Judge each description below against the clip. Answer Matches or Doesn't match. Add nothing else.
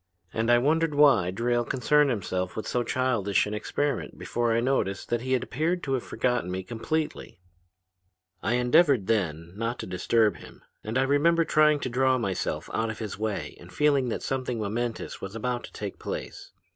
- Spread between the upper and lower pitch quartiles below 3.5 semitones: Doesn't match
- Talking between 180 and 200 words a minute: Matches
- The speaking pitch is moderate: Doesn't match